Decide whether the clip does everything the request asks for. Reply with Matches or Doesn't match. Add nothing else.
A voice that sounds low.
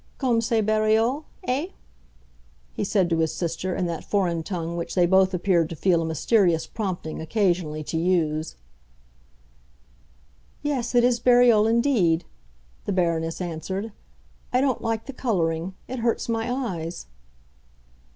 Doesn't match